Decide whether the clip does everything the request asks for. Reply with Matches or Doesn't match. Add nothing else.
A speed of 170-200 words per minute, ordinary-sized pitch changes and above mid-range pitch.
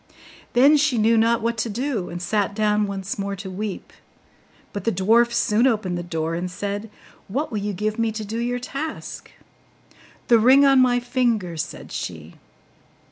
Matches